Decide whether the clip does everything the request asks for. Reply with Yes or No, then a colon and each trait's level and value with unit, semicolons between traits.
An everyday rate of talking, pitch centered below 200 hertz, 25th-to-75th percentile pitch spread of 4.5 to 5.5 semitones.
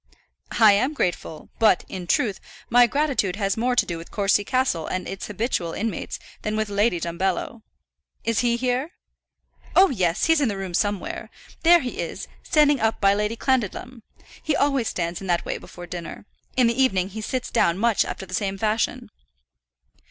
No: average, 180 wpm; high, 215 Hz; average, 4.9 semitones